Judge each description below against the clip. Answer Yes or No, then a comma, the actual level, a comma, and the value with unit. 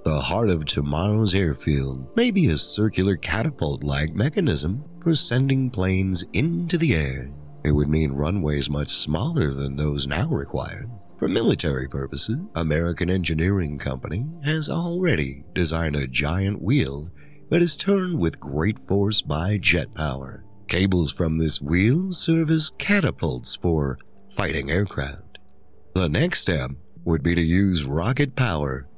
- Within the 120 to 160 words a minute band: Yes, average, 140 wpm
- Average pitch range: No, wide, 8.0 semitones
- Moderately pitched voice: No, very low, 85 Hz